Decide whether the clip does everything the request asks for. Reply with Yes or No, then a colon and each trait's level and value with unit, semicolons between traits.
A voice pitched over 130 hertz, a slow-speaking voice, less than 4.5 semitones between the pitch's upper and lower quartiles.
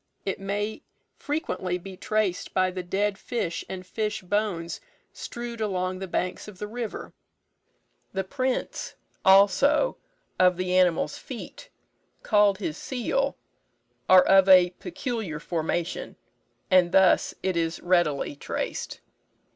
Yes: high, 190 Hz; slow, 125 wpm; average, 2.9 semitones